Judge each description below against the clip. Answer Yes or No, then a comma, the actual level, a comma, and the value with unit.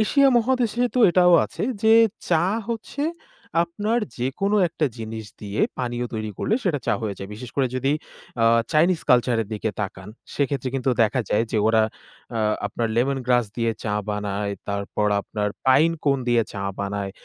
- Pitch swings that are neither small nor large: No, wide, 7.8 semitones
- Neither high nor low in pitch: No, low, 125 Hz